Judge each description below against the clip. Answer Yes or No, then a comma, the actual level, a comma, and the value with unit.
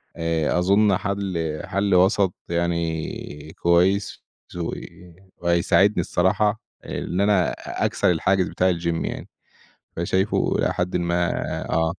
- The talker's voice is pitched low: Yes, very low, 90 Hz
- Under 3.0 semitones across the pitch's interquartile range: Yes, narrow, 2.4 semitones